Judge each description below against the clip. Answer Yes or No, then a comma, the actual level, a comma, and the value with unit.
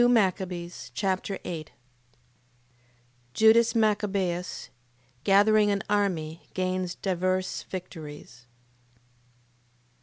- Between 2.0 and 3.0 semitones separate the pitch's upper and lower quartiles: Yes, average, 2.7 semitones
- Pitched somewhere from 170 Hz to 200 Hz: Yes, medium, 185 Hz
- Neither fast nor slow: No, slow, 70 wpm